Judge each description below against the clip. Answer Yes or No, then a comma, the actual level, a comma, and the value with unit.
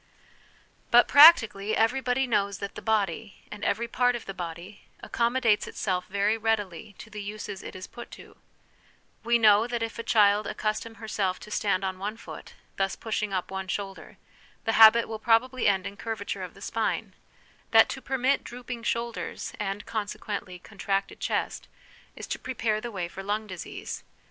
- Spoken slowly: No, average, 175 wpm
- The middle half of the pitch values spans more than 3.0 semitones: No, average, 2.7 semitones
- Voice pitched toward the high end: Yes, high, 215 Hz